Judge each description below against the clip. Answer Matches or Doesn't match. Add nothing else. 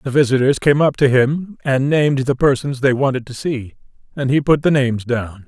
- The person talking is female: Doesn't match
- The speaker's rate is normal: Doesn't match